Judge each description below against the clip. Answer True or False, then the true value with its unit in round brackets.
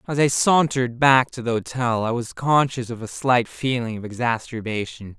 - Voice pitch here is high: False (120 Hz)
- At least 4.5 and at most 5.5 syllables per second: True (5.0 syllables/s)